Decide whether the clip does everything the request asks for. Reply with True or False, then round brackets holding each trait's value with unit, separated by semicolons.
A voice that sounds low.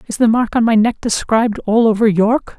False (225 Hz)